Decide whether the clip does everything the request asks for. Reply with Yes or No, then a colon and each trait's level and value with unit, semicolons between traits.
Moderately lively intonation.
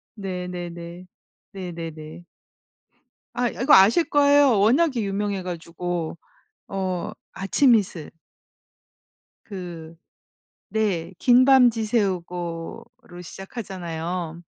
Yes: average, 4.4 semitones